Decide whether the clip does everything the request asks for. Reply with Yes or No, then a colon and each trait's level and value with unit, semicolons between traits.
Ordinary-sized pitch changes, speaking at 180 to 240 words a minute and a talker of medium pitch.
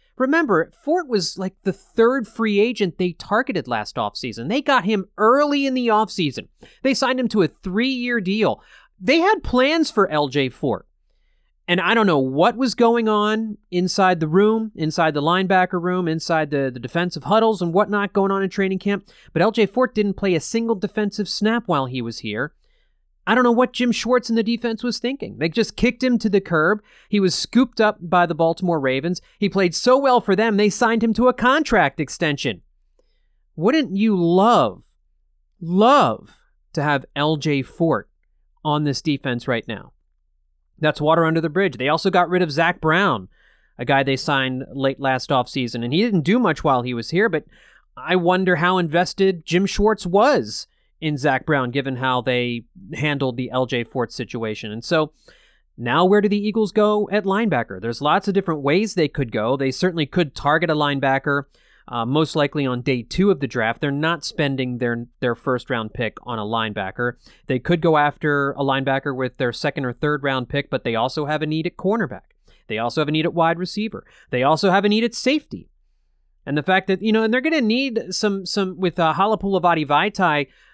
No: wide, 7.4 semitones; average, 200 wpm; medium, 175 Hz